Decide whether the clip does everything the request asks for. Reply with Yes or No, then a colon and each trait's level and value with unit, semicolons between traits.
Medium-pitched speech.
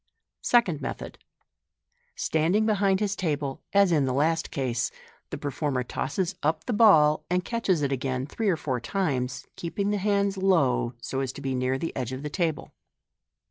Yes: medium, 155 Hz